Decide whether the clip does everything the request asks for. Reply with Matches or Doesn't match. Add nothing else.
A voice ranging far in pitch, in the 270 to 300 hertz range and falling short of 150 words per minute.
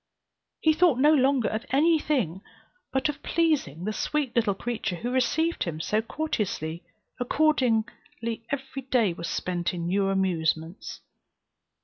Doesn't match